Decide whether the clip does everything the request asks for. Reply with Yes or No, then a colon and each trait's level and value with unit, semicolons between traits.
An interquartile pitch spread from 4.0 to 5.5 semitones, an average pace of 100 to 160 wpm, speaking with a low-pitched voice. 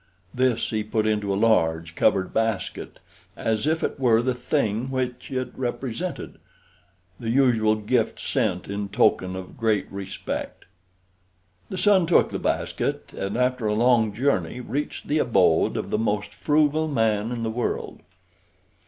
No: average, 3.6 semitones; average, 150 wpm; low, 115 Hz